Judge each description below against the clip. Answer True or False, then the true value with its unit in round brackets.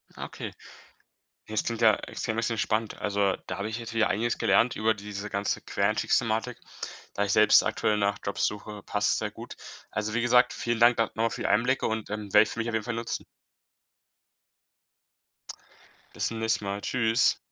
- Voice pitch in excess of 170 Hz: False (110 Hz)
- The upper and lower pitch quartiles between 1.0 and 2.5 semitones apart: True (1.8 semitones)